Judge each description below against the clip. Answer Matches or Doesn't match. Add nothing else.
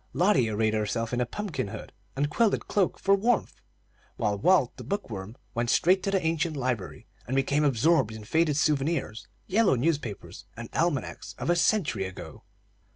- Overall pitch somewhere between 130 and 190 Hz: Matches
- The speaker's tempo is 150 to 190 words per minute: Matches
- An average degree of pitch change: Doesn't match